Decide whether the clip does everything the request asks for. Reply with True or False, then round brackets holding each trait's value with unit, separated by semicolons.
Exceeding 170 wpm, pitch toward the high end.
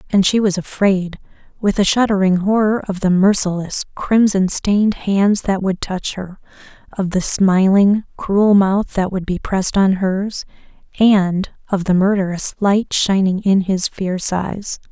False (155 wpm; 195 Hz)